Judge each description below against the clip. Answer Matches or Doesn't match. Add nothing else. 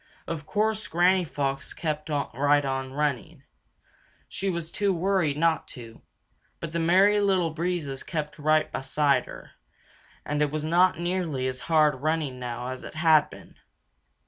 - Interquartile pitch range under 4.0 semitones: Matches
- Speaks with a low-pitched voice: Doesn't match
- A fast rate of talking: Doesn't match